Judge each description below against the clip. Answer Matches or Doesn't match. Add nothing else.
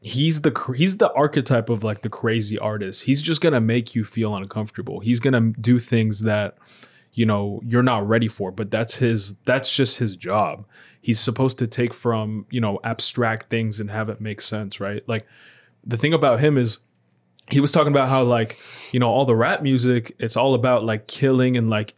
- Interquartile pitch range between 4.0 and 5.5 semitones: Doesn't match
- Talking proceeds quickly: Matches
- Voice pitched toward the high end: Doesn't match